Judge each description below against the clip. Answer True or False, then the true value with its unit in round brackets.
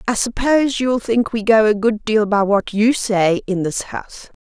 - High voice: True (220 Hz)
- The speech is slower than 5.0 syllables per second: True (4.6 syllables/s)